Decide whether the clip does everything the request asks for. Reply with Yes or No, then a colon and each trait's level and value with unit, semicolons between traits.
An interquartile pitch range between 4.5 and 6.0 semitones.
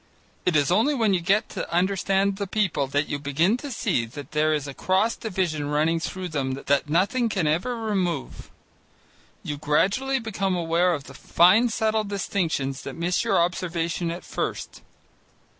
Yes: average, 4.9 semitones